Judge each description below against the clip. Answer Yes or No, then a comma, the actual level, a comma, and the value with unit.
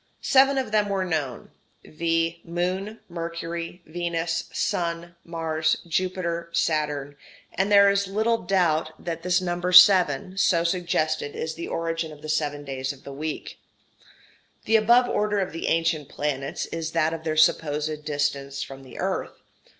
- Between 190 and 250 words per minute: No, average, 150 wpm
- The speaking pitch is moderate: Yes, medium, 165 Hz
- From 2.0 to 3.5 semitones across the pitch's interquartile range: Yes, average, 3.0 semitones